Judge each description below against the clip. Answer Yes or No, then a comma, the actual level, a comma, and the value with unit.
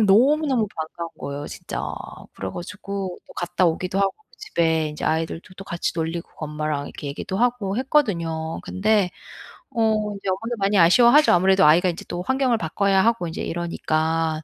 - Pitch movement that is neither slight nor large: Yes, average, 4.7 semitones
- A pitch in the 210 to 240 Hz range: No, medium, 185 Hz